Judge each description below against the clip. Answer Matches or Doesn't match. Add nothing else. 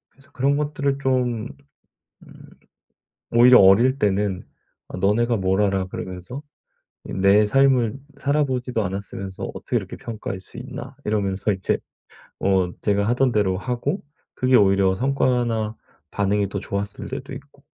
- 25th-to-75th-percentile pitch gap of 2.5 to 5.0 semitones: Matches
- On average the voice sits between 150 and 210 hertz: Doesn't match